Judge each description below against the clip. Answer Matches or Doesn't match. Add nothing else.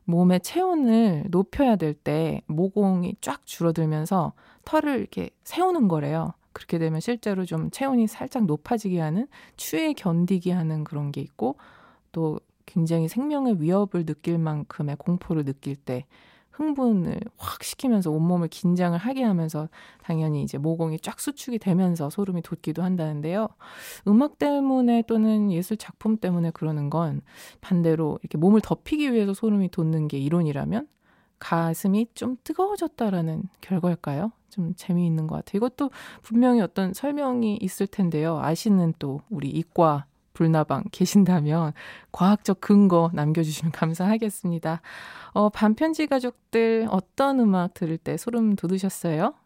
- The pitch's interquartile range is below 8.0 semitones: Matches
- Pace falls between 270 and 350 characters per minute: Matches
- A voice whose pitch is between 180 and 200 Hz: Matches